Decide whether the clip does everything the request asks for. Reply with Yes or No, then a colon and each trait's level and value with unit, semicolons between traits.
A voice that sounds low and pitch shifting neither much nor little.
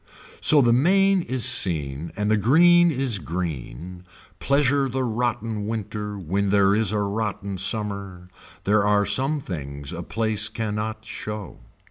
Yes: low, 105 Hz; average, 4.2 semitones